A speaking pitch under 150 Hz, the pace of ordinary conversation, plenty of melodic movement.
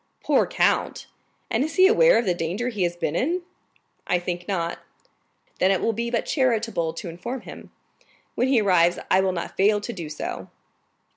No: high, 195 Hz; average, 190 wpm; wide, 5.7 semitones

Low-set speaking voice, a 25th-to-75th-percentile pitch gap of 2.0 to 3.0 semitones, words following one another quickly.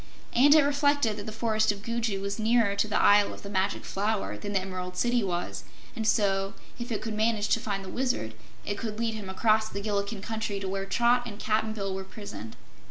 No: high, 210 Hz; narrow, 2.4 semitones; fast, 225 wpm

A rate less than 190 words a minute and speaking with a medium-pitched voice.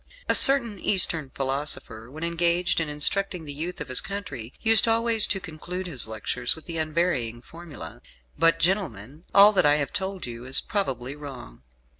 Yes: average, 170 wpm; medium, 160 Hz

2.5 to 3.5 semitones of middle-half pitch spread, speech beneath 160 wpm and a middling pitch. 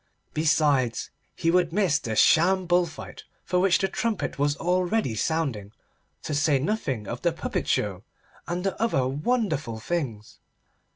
No: wide, 5.5 semitones; average, 150 wpm; medium, 160 Hz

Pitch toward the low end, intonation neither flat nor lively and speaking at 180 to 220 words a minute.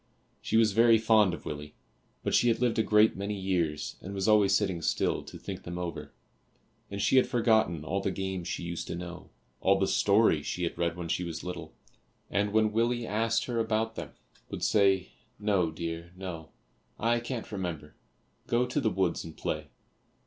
Yes: very low, 95 Hz; average, 4.4 semitones; average, 190 wpm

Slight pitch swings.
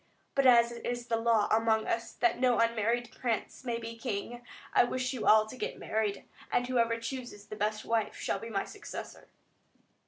Yes: narrow, 1.6 semitones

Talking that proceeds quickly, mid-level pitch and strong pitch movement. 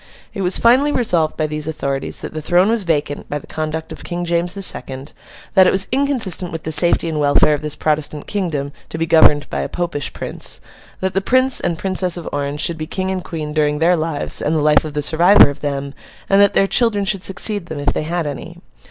No: fast, 235 wpm; medium, 165 Hz; average, 3.9 semitones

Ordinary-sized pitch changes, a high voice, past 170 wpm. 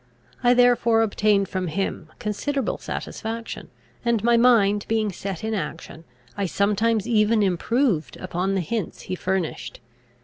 No: average, 3.4 semitones; high, 210 Hz; slow, 135 wpm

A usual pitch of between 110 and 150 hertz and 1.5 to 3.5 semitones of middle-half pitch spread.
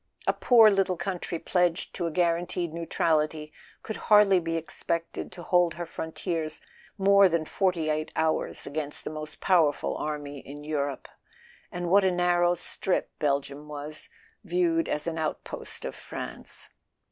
No: medium, 170 Hz; average, 2.9 semitones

